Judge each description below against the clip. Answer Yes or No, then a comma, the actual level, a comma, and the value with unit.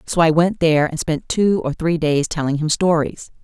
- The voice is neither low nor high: Yes, medium, 160 Hz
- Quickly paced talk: Yes, fast, 225 wpm